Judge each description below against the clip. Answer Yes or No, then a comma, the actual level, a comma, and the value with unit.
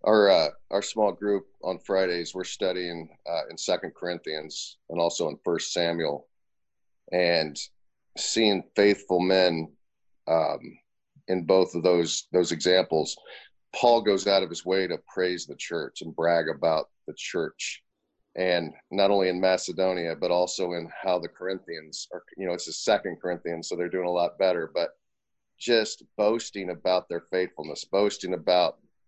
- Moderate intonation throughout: No, narrow, 1.9 semitones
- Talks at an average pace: Yes, average, 155 wpm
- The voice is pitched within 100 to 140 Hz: No, very low, 90 Hz